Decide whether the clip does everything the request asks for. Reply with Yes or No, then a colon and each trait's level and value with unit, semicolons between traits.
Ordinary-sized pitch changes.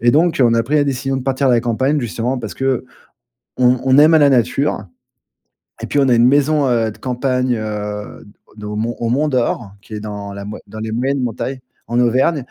Yes: average, 3.3 semitones